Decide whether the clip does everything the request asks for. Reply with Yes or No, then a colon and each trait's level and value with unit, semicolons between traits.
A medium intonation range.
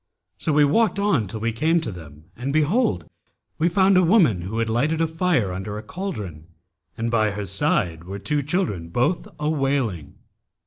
No: wide, 8.5 semitones